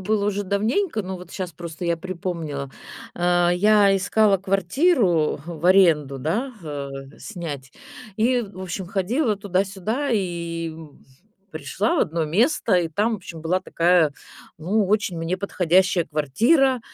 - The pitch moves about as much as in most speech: Yes, average, 3.8 semitones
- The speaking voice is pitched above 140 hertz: Yes, medium, 185 Hz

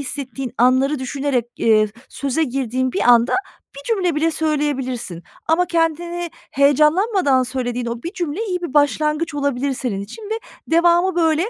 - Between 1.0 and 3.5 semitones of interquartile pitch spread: No, average, 4.6 semitones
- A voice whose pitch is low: No, very high, 290 Hz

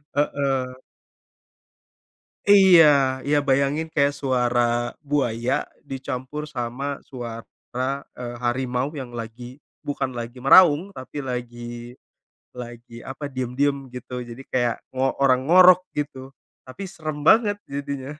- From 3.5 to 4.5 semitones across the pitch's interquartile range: No, average, 2.8 semitones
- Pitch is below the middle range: Yes, low, 130 Hz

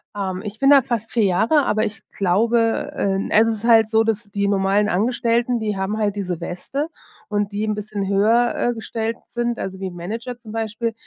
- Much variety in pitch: No, narrow, 2.6 semitones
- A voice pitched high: Yes, high, 215 Hz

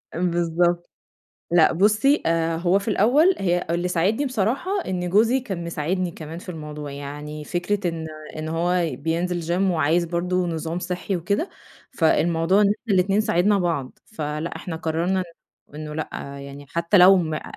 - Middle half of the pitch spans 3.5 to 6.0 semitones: No, average, 3.1 semitones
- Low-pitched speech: No, medium, 175 Hz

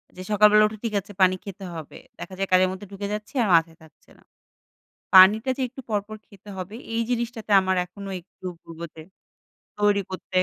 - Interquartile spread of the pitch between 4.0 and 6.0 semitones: No, narrow, 2.4 semitones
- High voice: Yes, high, 200 Hz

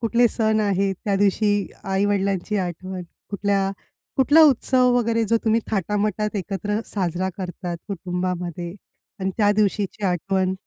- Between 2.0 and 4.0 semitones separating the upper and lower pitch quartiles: Yes, narrow, 2.4 semitones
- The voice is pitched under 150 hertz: No, high, 200 Hz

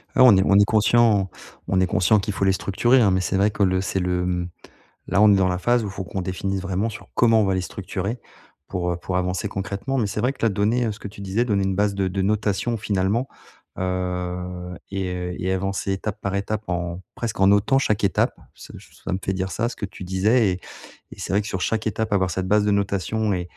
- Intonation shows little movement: Yes, narrow, 2.3 semitones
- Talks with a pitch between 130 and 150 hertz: No, very low, 95 Hz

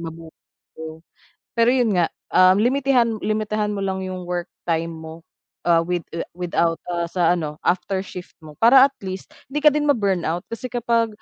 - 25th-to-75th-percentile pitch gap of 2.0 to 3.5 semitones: No, average, 5.3 semitones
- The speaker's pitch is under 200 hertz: Yes, medium, 185 Hz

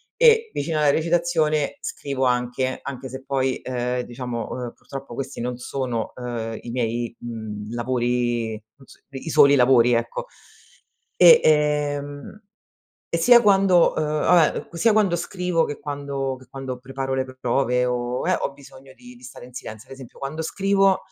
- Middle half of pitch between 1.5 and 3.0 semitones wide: No, average, 4.2 semitones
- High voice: No, low, 135 Hz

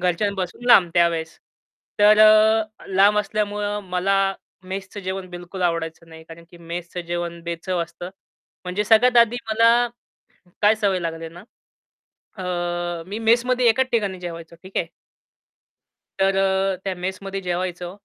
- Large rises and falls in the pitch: No, average, 3.2 semitones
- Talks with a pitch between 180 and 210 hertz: Yes, high, 190 Hz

